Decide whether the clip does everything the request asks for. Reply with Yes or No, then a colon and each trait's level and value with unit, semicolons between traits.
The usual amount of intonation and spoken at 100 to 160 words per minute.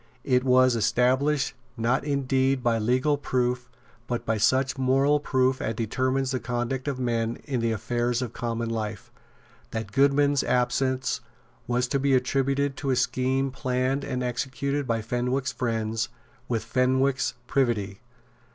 No: narrow, 2.2 semitones; average, 140 wpm